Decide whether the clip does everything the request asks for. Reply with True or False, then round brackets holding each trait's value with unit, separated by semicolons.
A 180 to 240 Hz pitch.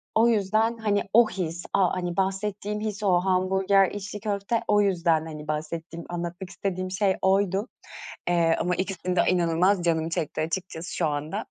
True (185 Hz)